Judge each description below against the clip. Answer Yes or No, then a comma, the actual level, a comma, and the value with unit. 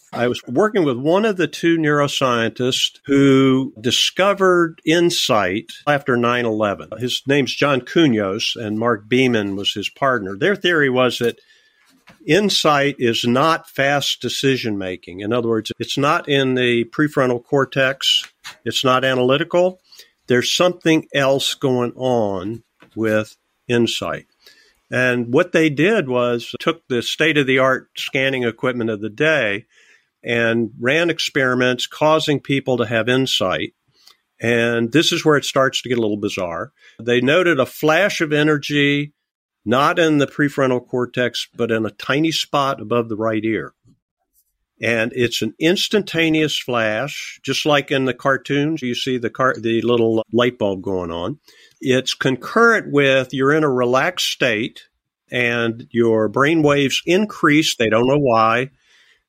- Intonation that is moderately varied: Yes, average, 4.0 semitones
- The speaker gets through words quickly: No, average, 145 wpm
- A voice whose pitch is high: No, low, 130 Hz